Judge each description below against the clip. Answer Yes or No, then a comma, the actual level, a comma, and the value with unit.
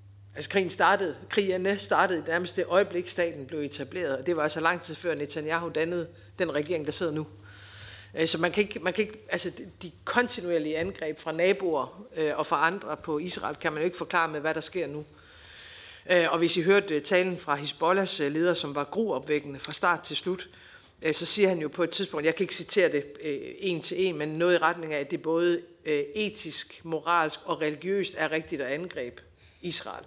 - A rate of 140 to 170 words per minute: No, average, 200 wpm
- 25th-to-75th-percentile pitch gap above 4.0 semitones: No, average, 3.0 semitones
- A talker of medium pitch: Yes, medium, 165 Hz